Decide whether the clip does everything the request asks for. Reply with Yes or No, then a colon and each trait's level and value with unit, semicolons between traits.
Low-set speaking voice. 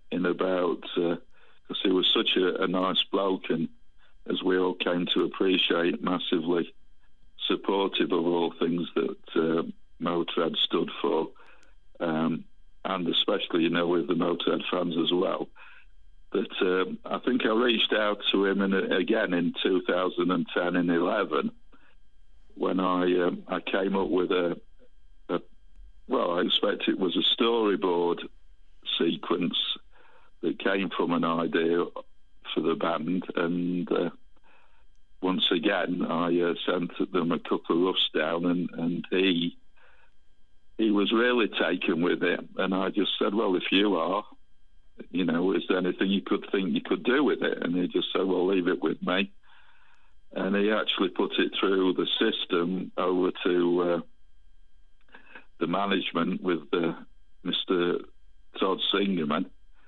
Yes: very low, 90 Hz